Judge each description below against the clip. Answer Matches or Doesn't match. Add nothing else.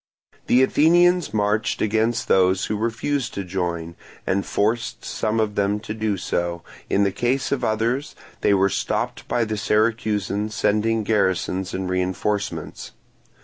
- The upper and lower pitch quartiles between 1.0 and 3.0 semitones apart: Matches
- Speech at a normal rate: Matches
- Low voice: Matches